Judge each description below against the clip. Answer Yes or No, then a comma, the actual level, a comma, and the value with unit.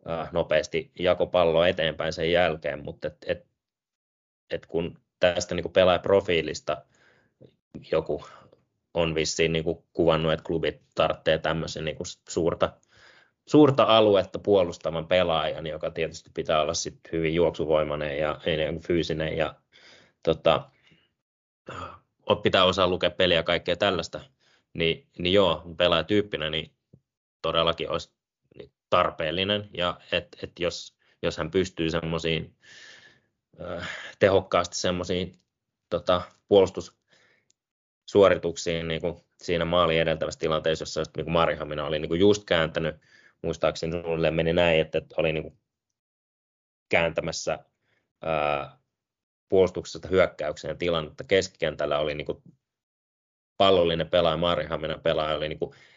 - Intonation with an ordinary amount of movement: No, narrow, 1.8 semitones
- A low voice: Yes, very low, 80 Hz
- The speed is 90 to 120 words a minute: Yes, average, 115 wpm